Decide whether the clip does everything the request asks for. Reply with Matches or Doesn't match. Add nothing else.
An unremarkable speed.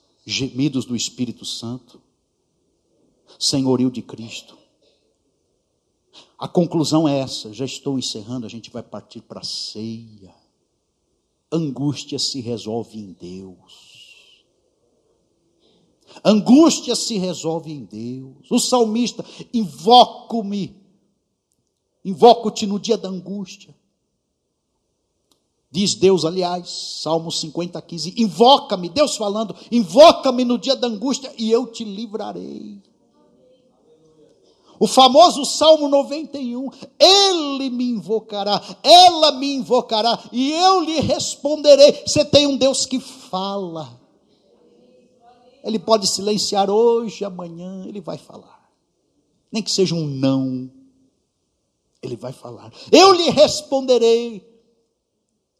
Doesn't match